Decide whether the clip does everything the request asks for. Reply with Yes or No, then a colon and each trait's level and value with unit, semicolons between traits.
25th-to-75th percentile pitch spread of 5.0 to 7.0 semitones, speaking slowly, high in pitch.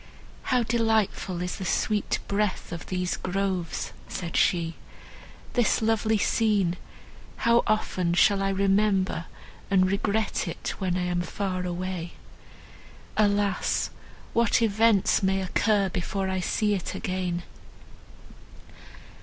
No: average, 2.8 semitones; slow, 110 wpm; high, 195 Hz